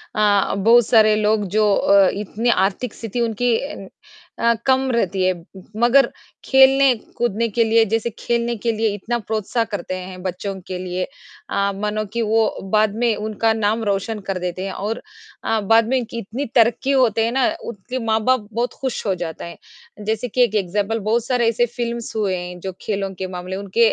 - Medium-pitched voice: No, high, 220 Hz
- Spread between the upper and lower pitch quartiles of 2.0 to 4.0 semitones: Yes, average, 3.0 semitones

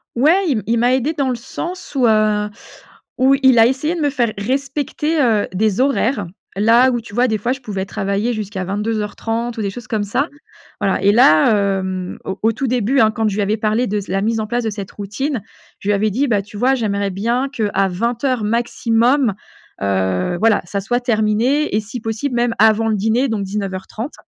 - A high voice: Yes, high, 225 Hz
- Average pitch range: Yes, average, 3.5 semitones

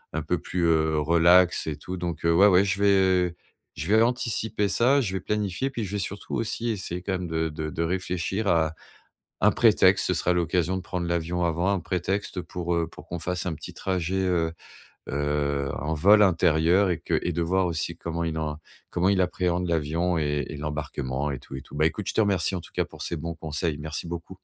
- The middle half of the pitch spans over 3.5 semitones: No, average, 2.9 semitones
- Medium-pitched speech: No, very low, 85 Hz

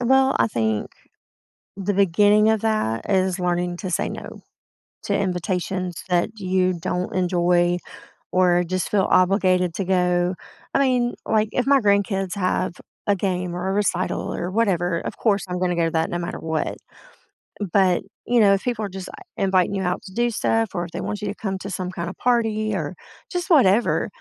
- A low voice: No, high, 190 Hz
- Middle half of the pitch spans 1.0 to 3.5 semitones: Yes, average, 2.8 semitones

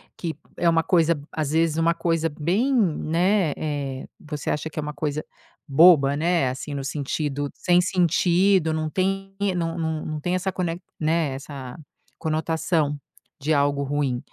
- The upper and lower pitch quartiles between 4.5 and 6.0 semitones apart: No, average, 2.9 semitones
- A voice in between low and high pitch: Yes, medium, 160 Hz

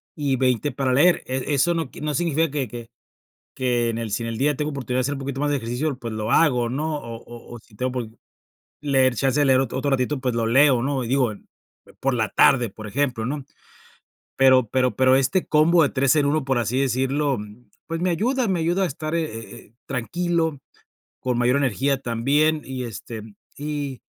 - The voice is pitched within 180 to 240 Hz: No, low, 135 Hz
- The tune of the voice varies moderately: Yes, average, 3.4 semitones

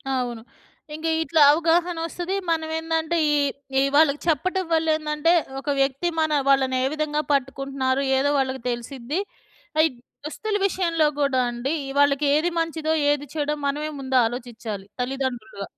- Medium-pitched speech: No, very high, 290 Hz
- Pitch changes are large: No, average, 3.5 semitones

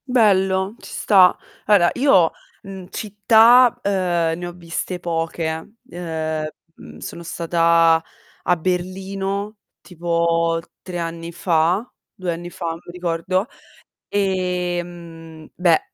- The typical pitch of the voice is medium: Yes, medium, 175 Hz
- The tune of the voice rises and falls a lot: No, narrow, 2.4 semitones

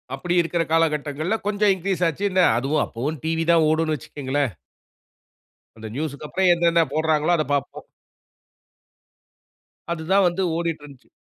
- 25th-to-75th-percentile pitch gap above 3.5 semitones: No, average, 2.8 semitones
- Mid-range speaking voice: Yes, medium, 160 Hz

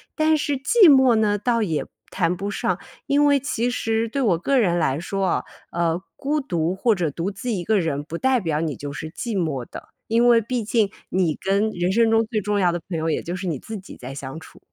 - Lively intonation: Yes, wide, 5.8 semitones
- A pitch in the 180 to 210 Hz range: Yes, high, 200 Hz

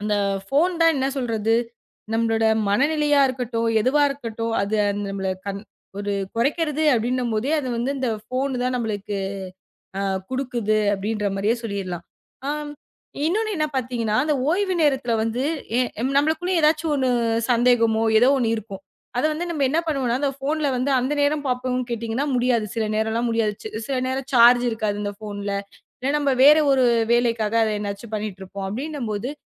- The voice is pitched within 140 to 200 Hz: No, high, 240 Hz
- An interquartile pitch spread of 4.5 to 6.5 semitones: No, average, 4.1 semitones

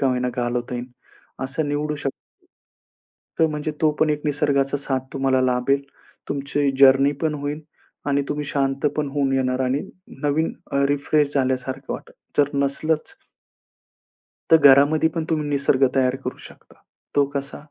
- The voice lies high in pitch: No, medium, 140 Hz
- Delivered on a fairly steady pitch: Yes, narrow, 1.8 semitones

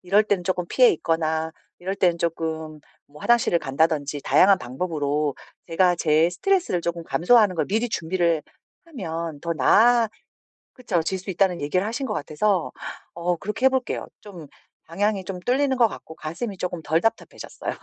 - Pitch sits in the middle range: Yes, medium, 175 Hz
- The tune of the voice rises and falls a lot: No, average, 4.5 semitones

